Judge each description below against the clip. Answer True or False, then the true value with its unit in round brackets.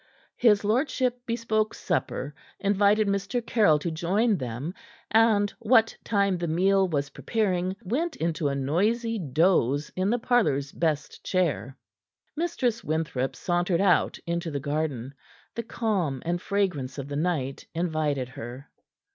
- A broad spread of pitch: True (6.6 semitones)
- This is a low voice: False (180 Hz)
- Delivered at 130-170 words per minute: True (135 wpm)